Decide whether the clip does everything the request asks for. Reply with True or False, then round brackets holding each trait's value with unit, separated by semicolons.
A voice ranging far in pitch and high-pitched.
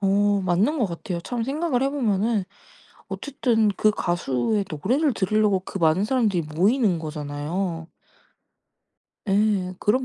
False (5.0 semitones; 200 Hz)